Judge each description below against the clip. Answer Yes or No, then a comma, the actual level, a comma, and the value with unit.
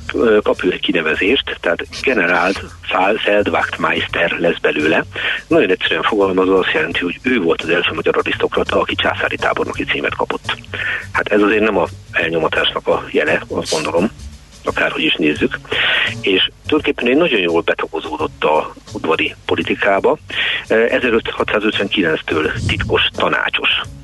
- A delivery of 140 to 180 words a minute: No, average, 125 wpm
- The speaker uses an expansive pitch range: Yes, wide, 6.5 semitones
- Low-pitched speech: Yes, very low, 95 Hz